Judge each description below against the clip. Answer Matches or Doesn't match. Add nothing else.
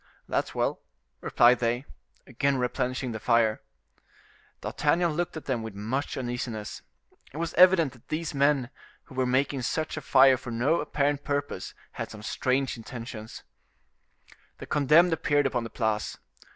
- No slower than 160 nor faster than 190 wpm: Doesn't match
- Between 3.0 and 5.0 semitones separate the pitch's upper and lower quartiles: Matches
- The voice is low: Matches